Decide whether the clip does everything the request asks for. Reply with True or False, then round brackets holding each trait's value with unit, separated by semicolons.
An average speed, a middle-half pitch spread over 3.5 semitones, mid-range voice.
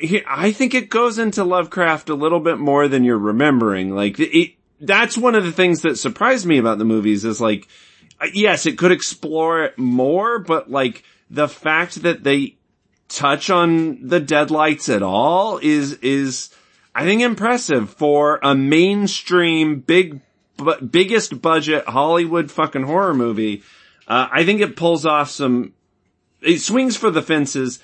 True (160 wpm; 5.1 semitones; 160 Hz)